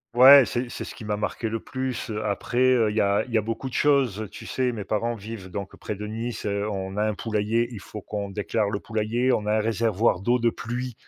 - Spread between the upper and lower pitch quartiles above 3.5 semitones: No, narrow, 2.5 semitones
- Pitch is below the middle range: Yes, low, 110 Hz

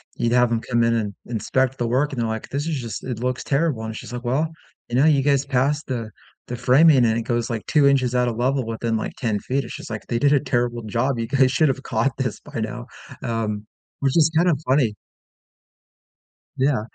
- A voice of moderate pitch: No, low, 125 Hz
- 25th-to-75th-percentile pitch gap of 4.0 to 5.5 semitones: No, average, 3.0 semitones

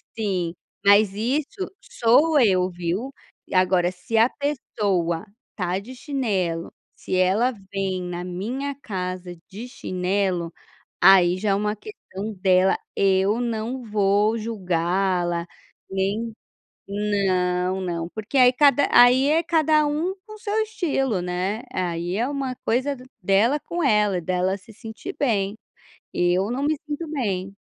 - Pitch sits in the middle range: No, high, 205 Hz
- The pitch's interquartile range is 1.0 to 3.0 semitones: No, wide, 5.5 semitones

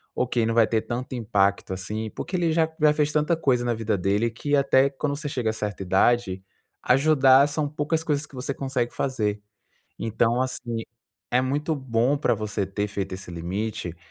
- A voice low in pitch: Yes, low, 120 Hz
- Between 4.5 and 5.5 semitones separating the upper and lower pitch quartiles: Yes, average, 5.0 semitones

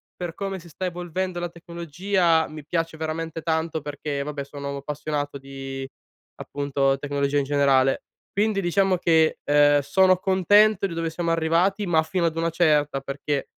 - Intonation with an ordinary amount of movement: Yes, average, 3.4 semitones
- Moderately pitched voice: Yes, medium, 160 Hz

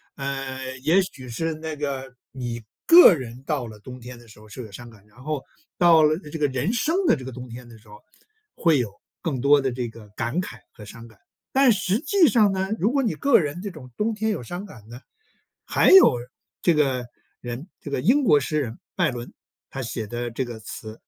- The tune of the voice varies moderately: No, wide, 6.3 semitones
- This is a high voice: No, low, 135 Hz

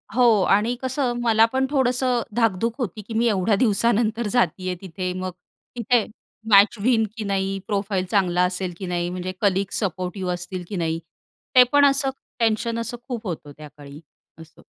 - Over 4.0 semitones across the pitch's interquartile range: Yes, average, 4.4 semitones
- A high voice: Yes, high, 200 Hz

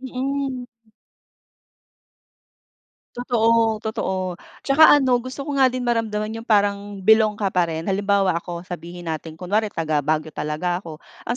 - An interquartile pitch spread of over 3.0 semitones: Yes, average, 5.3 semitones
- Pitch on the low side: No, high, 205 Hz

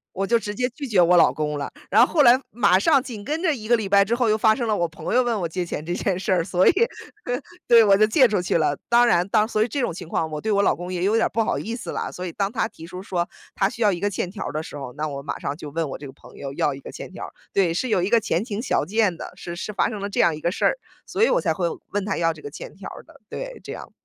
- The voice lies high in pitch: Yes, high, 200 Hz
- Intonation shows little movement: No, average, 5.0 semitones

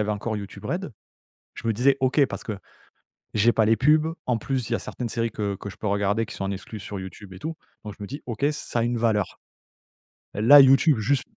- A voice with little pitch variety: No, average, 4.0 semitones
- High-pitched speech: No, low, 115 Hz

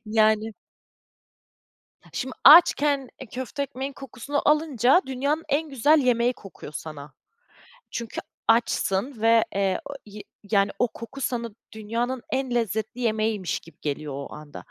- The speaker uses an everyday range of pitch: Yes, average, 4.1 semitones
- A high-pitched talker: Yes, high, 235 Hz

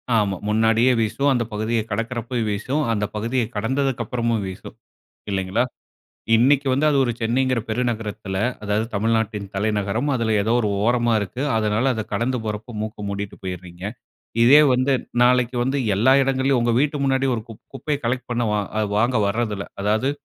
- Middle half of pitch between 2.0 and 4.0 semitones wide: Yes, average, 3.2 semitones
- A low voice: Yes, low, 115 Hz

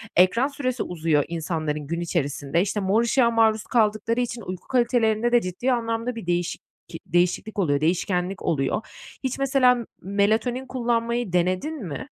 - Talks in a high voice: Yes, high, 215 Hz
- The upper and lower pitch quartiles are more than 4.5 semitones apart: Yes, wide, 5.5 semitones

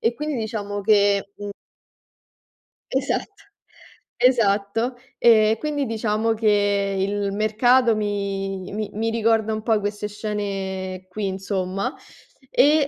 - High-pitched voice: Yes, high, 210 Hz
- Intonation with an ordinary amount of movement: No, narrow, 2.2 semitones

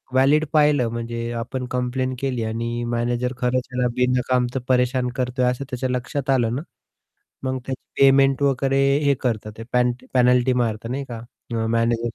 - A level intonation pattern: Yes, narrow, 1.8 semitones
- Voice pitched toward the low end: Yes, low, 125 Hz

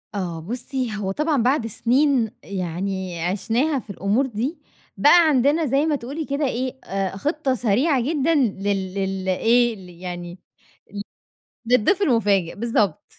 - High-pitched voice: Yes, high, 230 Hz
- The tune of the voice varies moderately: No, wide, 6.2 semitones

